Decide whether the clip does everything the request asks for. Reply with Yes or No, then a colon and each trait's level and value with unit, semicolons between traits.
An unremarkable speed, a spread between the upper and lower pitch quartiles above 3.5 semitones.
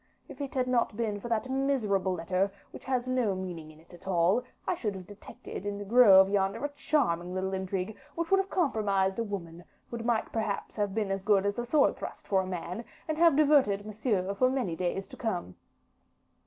No: fast, 210 wpm; average, 4.8 semitones